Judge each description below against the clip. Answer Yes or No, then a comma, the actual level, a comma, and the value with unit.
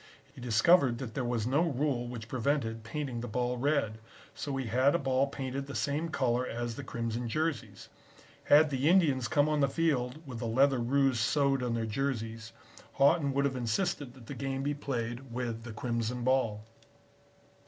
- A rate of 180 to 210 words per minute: Yes, average, 185 wpm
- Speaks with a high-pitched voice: No, low, 130 Hz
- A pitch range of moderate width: Yes, average, 3.1 semitones